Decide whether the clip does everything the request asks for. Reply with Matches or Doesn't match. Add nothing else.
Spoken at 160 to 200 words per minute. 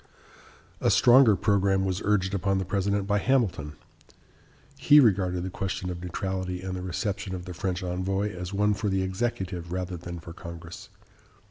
Matches